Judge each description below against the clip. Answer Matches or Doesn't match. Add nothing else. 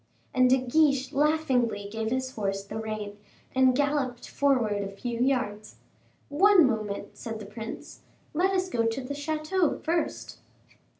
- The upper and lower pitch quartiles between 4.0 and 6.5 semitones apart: Matches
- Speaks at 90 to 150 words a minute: Matches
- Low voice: Doesn't match